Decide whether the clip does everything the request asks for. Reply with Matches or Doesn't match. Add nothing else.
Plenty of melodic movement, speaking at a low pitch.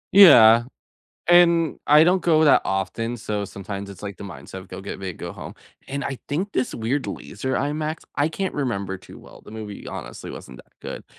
Matches